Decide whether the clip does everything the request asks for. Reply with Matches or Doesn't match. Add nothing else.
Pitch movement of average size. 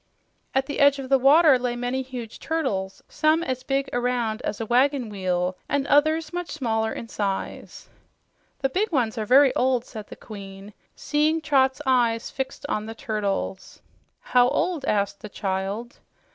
Matches